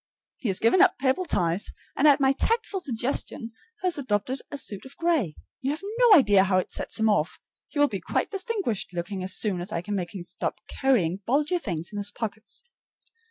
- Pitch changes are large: Yes, wide, 7.2 semitones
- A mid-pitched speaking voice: No, high, 225 Hz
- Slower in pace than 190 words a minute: No, fast, 205 wpm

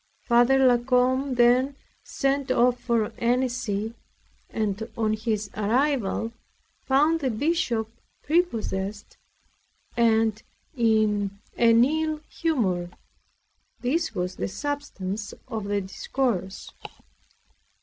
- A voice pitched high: Yes, high, 235 Hz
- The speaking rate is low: Yes, slow, 95 wpm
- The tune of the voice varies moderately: Yes, average, 4.0 semitones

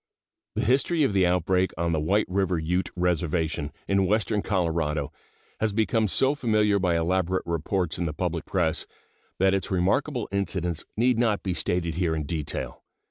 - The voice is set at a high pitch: No, very low, 90 Hz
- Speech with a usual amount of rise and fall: Yes, average, 3.7 semitones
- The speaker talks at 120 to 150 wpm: No, average, 165 wpm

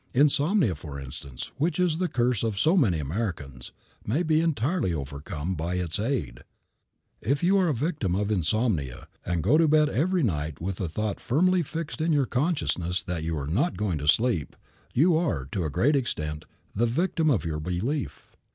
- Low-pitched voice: Yes, low, 110 Hz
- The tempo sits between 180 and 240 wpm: Yes, average, 185 wpm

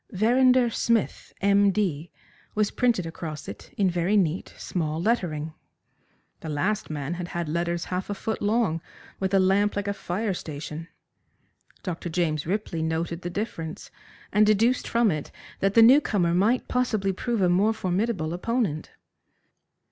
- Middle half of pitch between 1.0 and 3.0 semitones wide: No, average, 4.3 semitones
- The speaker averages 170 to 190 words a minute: No, average, 155 wpm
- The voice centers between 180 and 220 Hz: Yes, high, 190 Hz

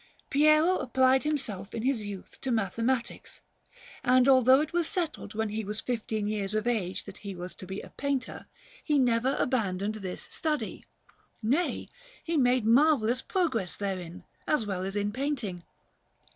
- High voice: Yes, high, 230 Hz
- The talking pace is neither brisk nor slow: Yes, average, 160 wpm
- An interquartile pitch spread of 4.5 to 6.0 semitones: Yes, average, 5.0 semitones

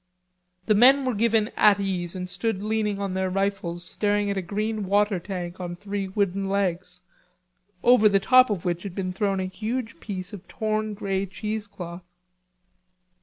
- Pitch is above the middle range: Yes, high, 200 Hz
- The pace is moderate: Yes, average, 170 wpm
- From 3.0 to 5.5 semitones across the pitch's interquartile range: No, narrow, 2.4 semitones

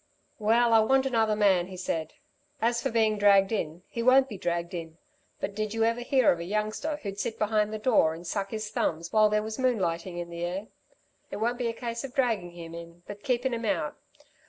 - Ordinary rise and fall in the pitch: Yes, average, 4.8 semitones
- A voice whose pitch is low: No, high, 210 Hz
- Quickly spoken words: Yes, fast, 225 wpm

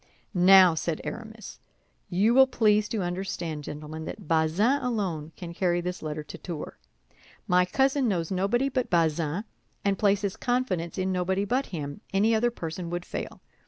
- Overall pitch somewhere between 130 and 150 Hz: No, medium, 185 Hz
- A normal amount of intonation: Yes, average, 4.6 semitones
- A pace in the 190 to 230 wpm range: No, average, 160 wpm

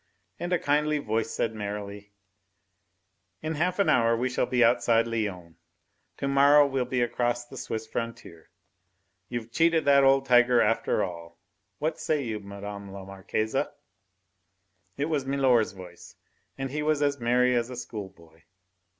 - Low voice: Yes, low, 120 Hz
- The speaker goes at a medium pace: Yes, average, 155 wpm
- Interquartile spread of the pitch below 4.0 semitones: No, average, 5.0 semitones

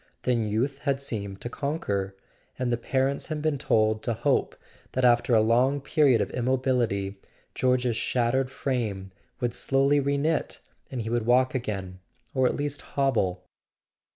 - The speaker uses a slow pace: No, average, 155 wpm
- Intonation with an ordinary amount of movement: Yes, average, 3.6 semitones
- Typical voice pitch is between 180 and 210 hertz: No, low, 125 Hz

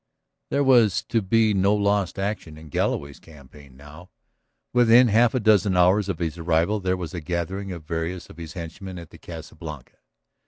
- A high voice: No, very low, 90 Hz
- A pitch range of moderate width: Yes, average, 4.2 semitones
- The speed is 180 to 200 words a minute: Yes, average, 185 wpm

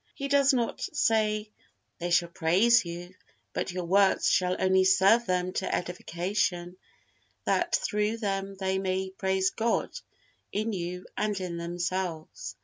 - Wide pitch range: No, average, 2.9 semitones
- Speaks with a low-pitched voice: No, high, 190 Hz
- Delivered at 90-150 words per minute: Yes, average, 140 wpm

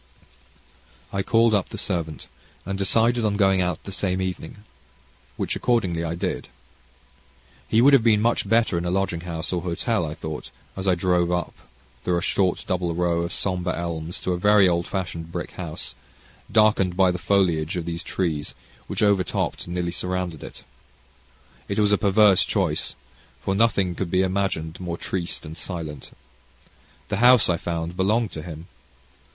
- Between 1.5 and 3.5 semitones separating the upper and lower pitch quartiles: Yes, narrow, 2.6 semitones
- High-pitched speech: No, very low, 90 Hz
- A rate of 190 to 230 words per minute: No, average, 170 wpm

